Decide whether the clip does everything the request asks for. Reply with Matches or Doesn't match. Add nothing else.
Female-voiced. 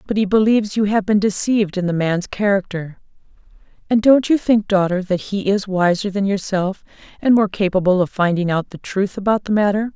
Matches